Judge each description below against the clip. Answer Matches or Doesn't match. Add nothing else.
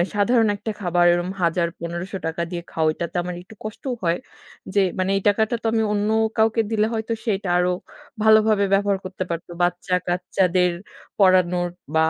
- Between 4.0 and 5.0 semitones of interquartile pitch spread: Doesn't match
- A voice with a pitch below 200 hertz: Matches